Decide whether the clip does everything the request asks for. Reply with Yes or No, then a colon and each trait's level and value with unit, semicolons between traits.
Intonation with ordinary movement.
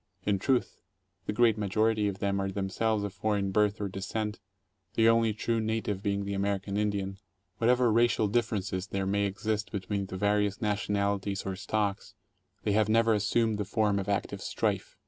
No: narrow, 1.8 semitones